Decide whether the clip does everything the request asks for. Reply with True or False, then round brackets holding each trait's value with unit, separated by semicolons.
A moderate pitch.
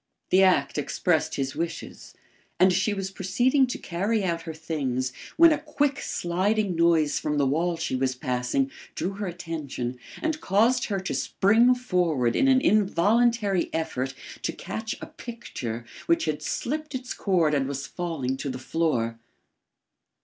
True (175 Hz)